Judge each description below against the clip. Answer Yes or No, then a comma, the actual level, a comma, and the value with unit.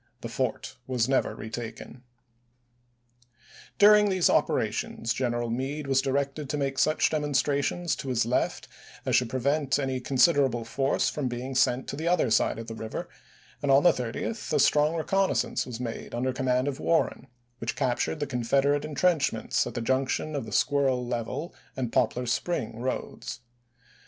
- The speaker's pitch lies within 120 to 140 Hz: Yes, low, 135 Hz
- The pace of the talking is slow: No, average, 160 wpm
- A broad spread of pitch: No, average, 3.1 semitones